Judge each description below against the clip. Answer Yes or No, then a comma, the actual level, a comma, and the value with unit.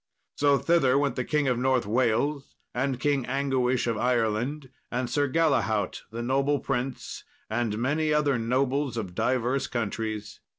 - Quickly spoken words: No, average, 145 wpm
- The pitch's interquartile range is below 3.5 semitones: Yes, average, 2.9 semitones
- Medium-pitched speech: No, low, 130 Hz